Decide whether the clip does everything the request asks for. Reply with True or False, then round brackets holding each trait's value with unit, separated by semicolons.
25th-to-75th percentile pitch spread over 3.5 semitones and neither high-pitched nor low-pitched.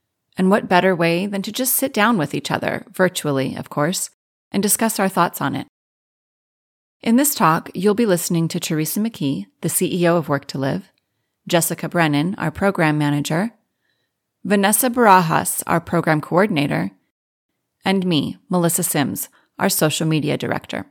True (4.1 semitones; 175 Hz)